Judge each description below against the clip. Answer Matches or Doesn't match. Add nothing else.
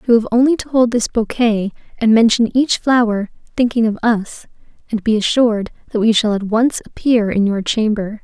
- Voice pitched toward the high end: Matches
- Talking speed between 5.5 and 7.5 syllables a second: Doesn't match